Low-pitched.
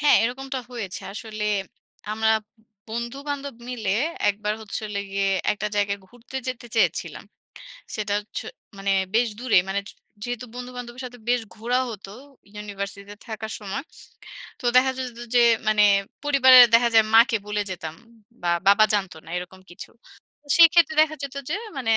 No: high, 225 Hz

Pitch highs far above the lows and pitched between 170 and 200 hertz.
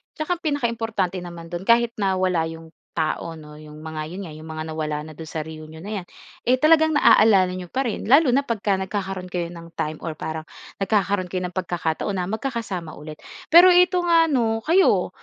Yes: wide, 6.5 semitones; medium, 185 Hz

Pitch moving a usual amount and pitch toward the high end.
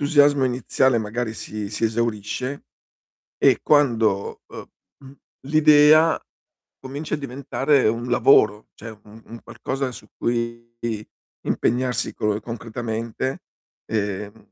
No: average, 3.8 semitones; low, 120 Hz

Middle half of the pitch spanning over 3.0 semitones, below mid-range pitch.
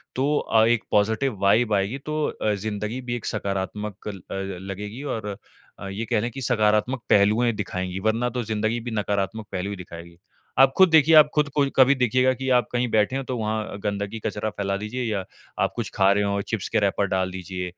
Yes: average, 3.6 semitones; low, 110 Hz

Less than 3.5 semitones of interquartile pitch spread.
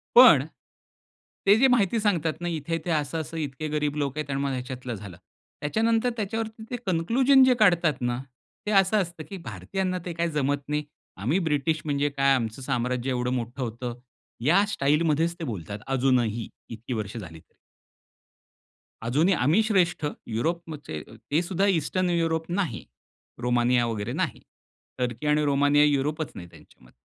No: wide, 5.6 semitones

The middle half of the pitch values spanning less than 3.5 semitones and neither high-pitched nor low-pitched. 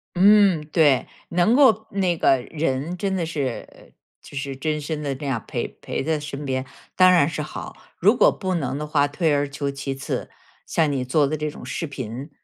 No: average, 3.9 semitones; medium, 150 Hz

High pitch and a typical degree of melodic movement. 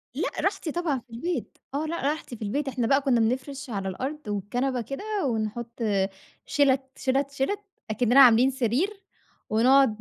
Yes: very high, 265 Hz; average, 3.4 semitones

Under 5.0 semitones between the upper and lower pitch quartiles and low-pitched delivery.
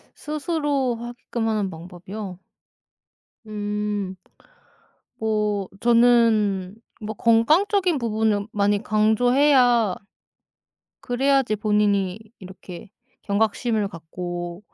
No: average, 3.3 semitones; high, 215 Hz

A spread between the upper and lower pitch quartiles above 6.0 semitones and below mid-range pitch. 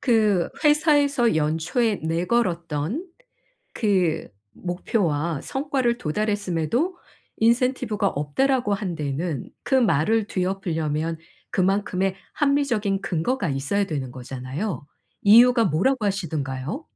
No: wide, 6.9 semitones; high, 195 Hz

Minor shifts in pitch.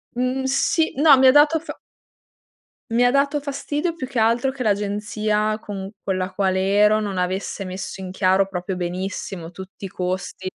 No: wide, 5.8 semitones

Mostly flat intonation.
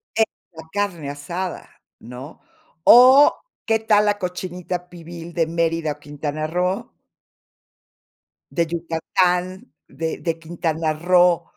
Yes: narrow, 2.2 semitones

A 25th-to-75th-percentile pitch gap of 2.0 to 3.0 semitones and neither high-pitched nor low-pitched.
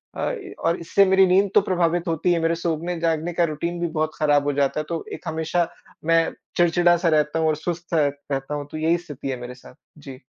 Yes: narrow, 2.4 semitones; medium, 165 Hz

